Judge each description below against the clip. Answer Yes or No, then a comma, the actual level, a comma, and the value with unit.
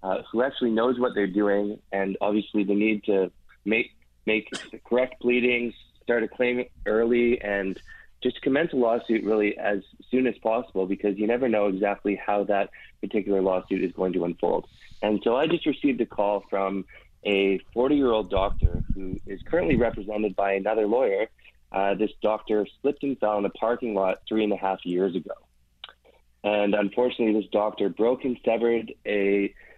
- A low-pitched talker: Yes, low, 105 Hz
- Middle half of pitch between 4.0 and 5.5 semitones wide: No, average, 3.2 semitones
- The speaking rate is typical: Yes, average, 175 wpm